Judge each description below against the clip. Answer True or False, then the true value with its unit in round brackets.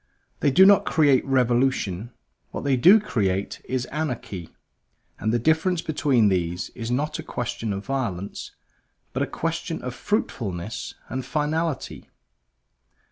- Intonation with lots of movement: True (6.1 semitones)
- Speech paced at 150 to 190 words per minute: False (135 wpm)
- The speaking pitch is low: True (125 Hz)